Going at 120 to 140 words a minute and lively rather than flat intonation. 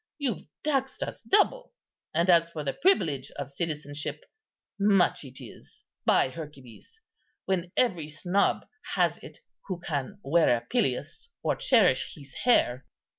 Yes: slow, 135 wpm; wide, 6.3 semitones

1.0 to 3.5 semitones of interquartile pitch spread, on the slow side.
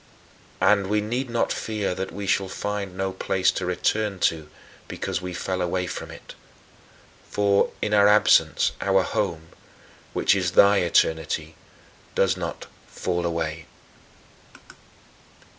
Yes: average, 2.8 semitones; slow, 130 wpm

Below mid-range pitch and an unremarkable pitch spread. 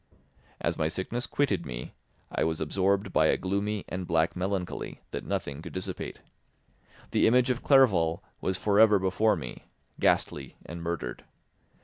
Yes: very low, 95 Hz; average, 4.2 semitones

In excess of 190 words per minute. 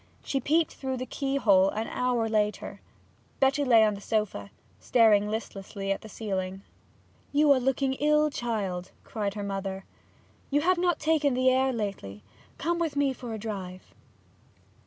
No: average, 155 wpm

